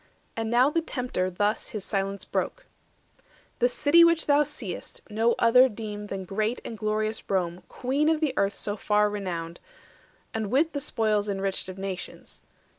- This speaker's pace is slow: No, average, 165 wpm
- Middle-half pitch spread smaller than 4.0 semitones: No, average, 4.4 semitones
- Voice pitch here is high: Yes, high, 215 Hz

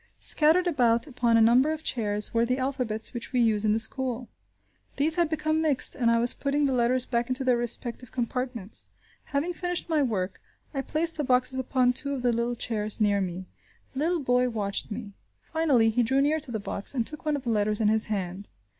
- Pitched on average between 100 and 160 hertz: No, very high, 250 Hz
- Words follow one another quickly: Yes, fast, 215 wpm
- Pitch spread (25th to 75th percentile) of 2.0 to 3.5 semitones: No, average, 3.9 semitones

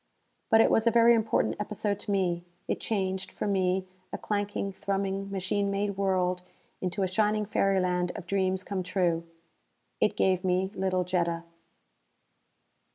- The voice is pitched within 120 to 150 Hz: No, high, 190 Hz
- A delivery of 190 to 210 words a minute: No, average, 150 wpm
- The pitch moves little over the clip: Yes, narrow, 1.8 semitones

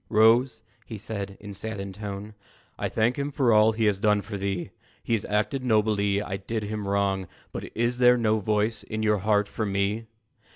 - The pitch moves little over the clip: Yes, narrow, 1.9 semitones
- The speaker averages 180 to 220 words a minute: Yes, average, 200 wpm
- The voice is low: Yes, low, 105 Hz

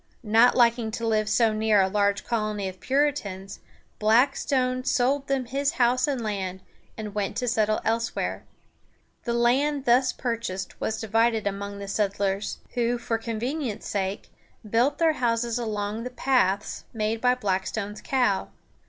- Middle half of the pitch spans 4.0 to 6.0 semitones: No, average, 3.3 semitones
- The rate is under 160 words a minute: Yes, average, 145 wpm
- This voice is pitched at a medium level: No, high, 230 Hz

